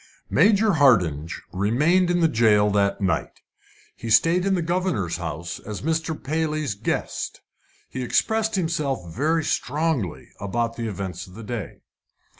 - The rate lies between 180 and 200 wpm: No, average, 140 wpm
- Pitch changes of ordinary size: No, wide, 8.5 semitones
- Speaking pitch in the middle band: No, low, 125 Hz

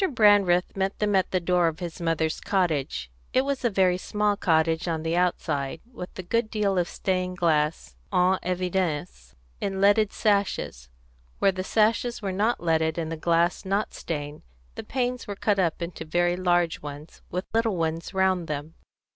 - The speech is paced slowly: No, average, 175 wpm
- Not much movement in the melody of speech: No, average, 3.4 semitones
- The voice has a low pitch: No, medium, 180 Hz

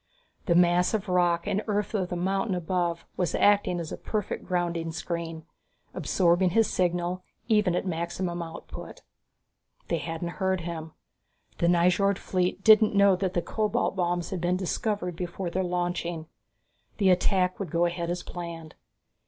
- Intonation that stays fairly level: Yes, narrow, 1.8 semitones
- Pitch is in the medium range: Yes, medium, 180 Hz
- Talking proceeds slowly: No, average, 155 wpm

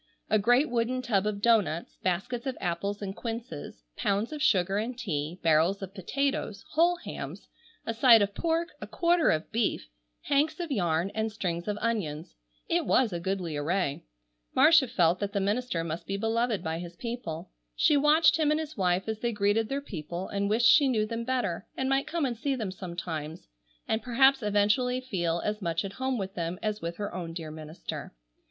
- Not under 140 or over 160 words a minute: No, average, 195 wpm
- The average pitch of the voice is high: Yes, high, 210 Hz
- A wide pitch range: Yes, wide, 6.1 semitones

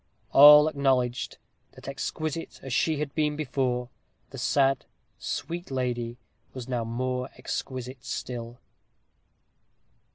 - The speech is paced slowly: Yes, slow, 105 wpm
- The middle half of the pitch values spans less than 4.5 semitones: Yes, average, 2.9 semitones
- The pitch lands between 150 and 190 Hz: No, low, 130 Hz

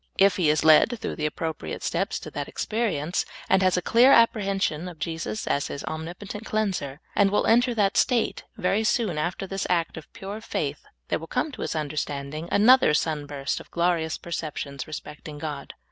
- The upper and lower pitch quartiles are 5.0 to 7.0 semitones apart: Yes, average, 5.3 semitones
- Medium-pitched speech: Yes, medium, 175 Hz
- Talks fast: No, average, 190 wpm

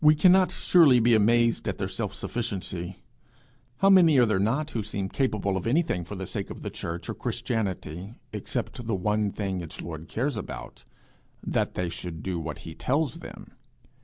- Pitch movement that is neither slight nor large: No, wide, 6.0 semitones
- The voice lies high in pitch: No, low, 110 Hz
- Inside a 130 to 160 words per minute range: No, average, 185 wpm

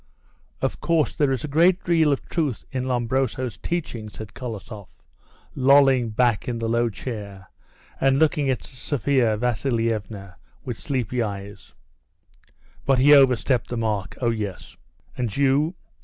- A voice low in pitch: Yes, low, 125 Hz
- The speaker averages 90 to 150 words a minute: Yes, average, 140 wpm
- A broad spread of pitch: No, average, 4.0 semitones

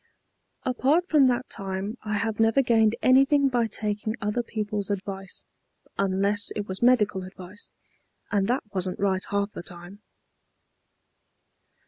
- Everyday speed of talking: No, slow, 130 wpm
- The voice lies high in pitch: Yes, high, 210 Hz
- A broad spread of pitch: No, average, 3.6 semitones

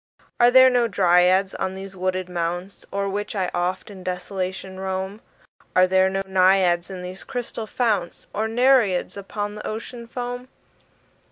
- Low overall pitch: No, high, 190 Hz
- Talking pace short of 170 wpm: Yes, average, 155 wpm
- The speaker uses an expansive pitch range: No, average, 2.9 semitones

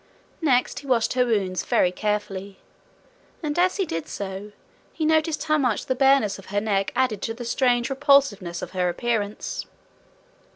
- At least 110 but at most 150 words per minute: No, average, 165 wpm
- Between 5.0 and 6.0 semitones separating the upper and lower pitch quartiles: Yes, wide, 5.6 semitones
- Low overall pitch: No, high, 230 Hz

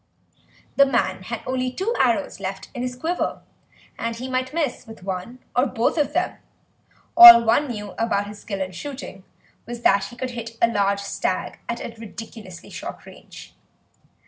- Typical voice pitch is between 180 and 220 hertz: No, high, 235 Hz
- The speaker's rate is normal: Yes, average, 170 wpm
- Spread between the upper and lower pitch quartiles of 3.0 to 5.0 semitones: Yes, average, 3.8 semitones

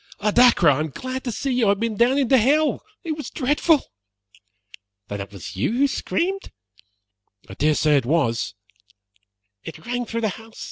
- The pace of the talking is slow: No, average, 185 wpm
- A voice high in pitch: Yes, high, 230 Hz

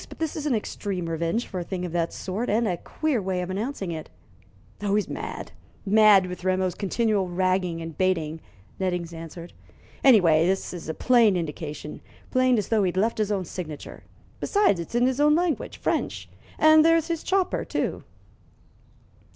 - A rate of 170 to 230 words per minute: Yes, average, 175 wpm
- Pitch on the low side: No, high, 190 Hz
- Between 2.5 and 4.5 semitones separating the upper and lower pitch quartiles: No, average, 5.3 semitones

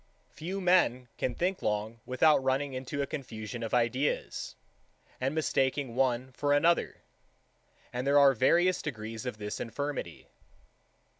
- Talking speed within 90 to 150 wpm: Yes, average, 140 wpm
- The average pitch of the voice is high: No, low, 130 Hz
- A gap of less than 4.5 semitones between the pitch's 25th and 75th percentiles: Yes, average, 3.3 semitones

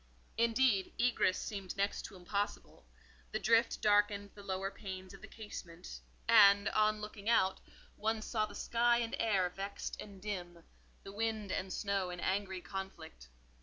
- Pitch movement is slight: Yes, narrow, 2.3 semitones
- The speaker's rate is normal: Yes, average, 155 wpm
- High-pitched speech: Yes, high, 200 Hz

